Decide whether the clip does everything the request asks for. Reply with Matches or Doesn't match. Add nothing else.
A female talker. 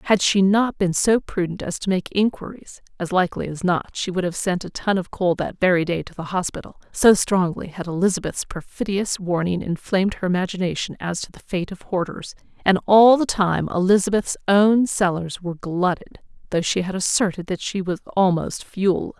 Matches